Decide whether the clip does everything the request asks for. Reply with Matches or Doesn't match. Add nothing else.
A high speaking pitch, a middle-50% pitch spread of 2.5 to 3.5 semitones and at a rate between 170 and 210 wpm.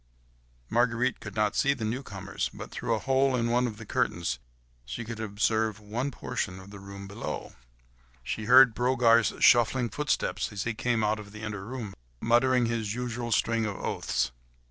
Doesn't match